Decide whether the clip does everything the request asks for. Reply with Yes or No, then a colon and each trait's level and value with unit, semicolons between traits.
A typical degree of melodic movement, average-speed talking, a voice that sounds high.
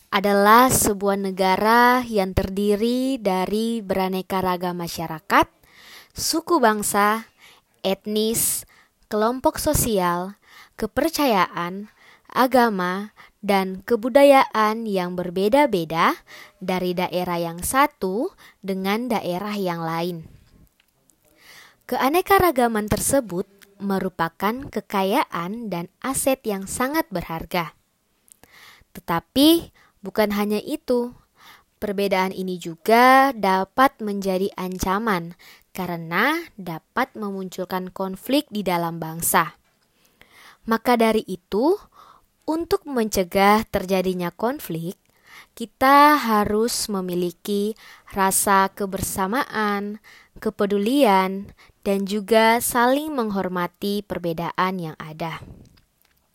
No: average, 4.1 semitones; slow, 80 wpm; high, 205 Hz